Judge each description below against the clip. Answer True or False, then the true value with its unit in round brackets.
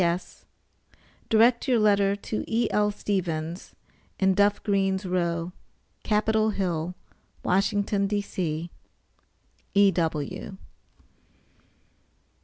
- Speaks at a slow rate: True (75 wpm)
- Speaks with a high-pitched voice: True (195 Hz)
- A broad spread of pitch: False (2.9 semitones)